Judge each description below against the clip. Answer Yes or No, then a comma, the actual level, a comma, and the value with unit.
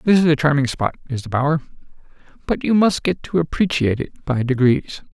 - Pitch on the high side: No, medium, 145 Hz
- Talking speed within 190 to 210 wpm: Yes, average, 200 wpm